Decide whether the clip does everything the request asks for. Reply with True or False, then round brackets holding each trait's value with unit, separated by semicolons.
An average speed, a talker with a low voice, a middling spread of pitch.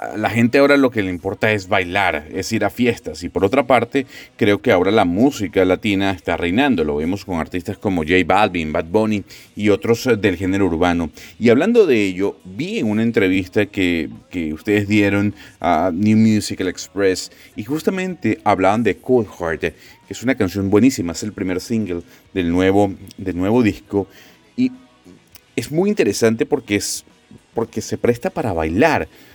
True (175 wpm; 100 Hz; 3.8 semitones)